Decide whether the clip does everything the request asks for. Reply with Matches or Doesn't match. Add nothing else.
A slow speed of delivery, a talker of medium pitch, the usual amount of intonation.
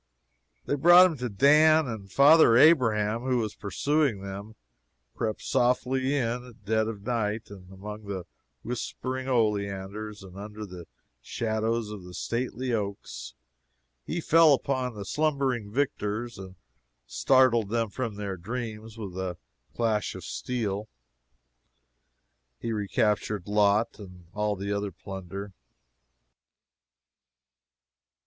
Doesn't match